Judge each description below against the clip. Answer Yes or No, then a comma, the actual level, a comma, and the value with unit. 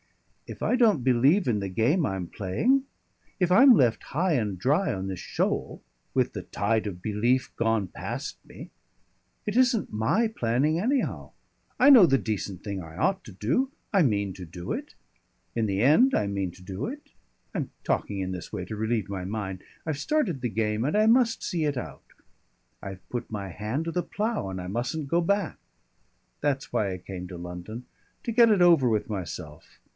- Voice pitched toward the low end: Yes, low, 115 Hz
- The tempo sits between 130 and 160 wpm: No, average, 190 wpm